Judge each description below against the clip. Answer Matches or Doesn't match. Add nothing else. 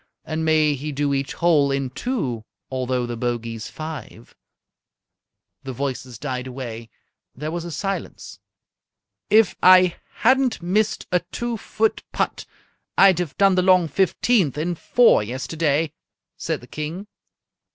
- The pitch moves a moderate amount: Doesn't match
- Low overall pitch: Doesn't match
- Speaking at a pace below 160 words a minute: Matches